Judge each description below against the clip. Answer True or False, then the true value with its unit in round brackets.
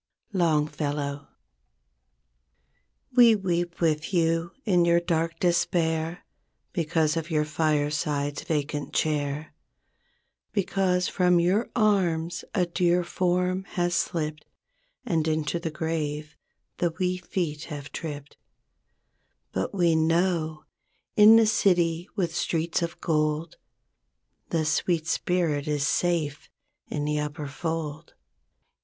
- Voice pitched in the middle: True (165 Hz)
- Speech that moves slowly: True (110 wpm)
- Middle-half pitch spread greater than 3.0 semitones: False (2.5 semitones)